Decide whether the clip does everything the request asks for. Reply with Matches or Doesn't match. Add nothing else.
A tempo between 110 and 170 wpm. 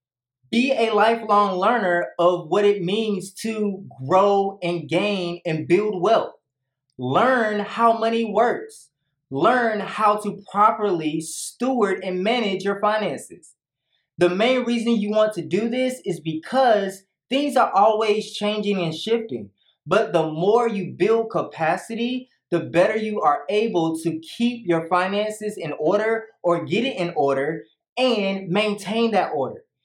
Matches